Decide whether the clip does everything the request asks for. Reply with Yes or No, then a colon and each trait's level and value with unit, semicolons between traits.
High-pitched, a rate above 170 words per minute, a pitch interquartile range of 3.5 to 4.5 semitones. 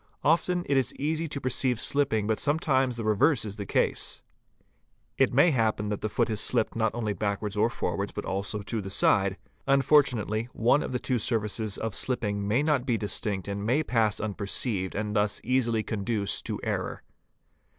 No: low, 115 Hz; average, 195 wpm; average, 4.1 semitones